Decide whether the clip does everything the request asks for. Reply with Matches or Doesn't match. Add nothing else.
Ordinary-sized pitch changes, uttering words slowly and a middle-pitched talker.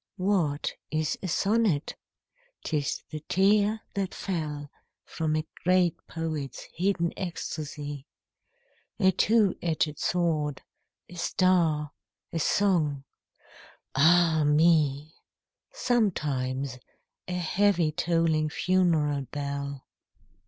Matches